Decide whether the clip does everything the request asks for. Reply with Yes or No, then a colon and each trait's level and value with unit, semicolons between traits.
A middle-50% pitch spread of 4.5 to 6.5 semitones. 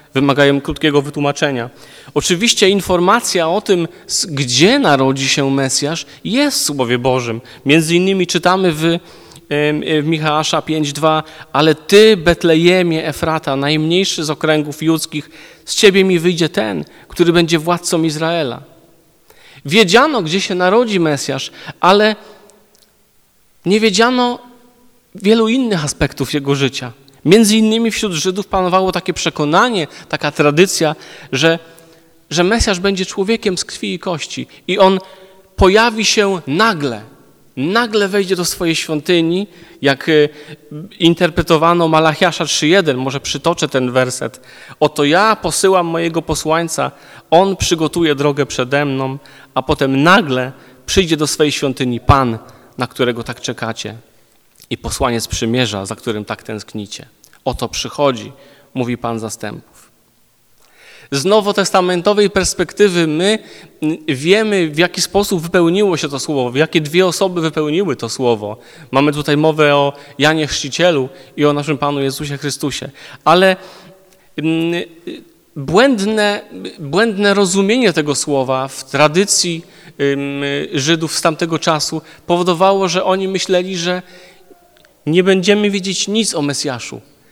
Yes: average, 5.0 semitones